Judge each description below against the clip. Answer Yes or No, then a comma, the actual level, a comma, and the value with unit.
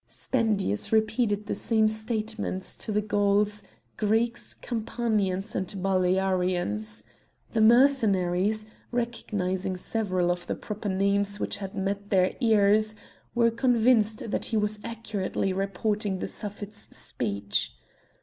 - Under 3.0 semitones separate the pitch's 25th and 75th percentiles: Yes, narrow, 2.6 semitones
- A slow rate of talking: Yes, slow, 115 wpm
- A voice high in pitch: Yes, high, 205 Hz